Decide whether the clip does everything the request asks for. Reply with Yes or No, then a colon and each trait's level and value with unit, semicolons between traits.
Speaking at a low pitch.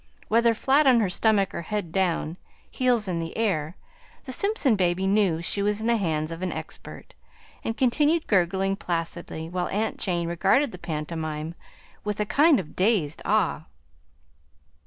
No: high, 195 Hz